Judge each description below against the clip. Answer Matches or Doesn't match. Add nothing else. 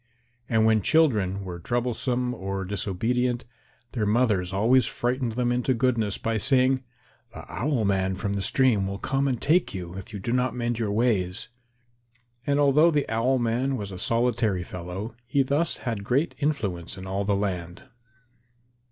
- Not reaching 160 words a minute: Doesn't match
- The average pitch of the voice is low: Matches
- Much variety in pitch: Doesn't match